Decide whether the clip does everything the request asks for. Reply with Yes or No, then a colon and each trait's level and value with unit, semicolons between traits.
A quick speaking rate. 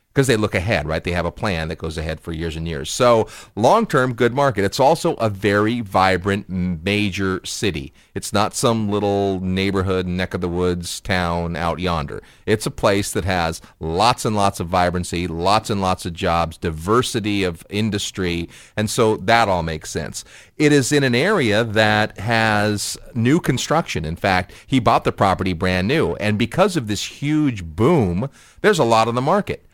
No: average, 190 wpm